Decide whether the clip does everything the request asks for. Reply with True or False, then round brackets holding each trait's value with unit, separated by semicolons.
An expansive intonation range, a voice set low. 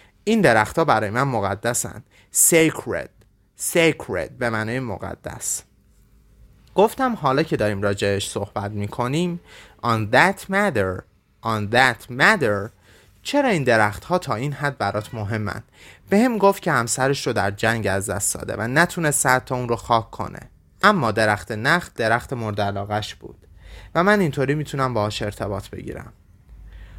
True (6.7 semitones; 115 Hz)